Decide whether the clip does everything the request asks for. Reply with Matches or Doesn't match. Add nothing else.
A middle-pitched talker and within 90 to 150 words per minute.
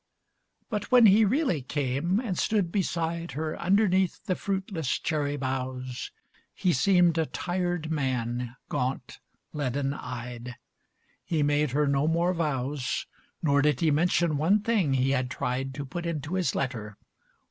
Matches